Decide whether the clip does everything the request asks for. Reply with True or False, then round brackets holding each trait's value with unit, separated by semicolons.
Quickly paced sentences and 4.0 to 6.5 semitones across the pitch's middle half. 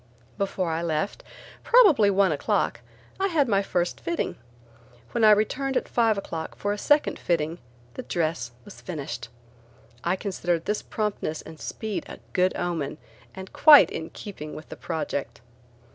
False (155 wpm; 4.9 semitones)